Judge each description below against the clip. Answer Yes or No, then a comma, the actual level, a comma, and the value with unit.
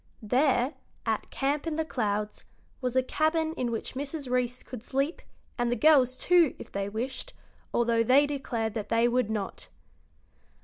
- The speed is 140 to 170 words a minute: Yes, average, 165 wpm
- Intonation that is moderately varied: Yes, average, 3.8 semitones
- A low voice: No, very high, 255 Hz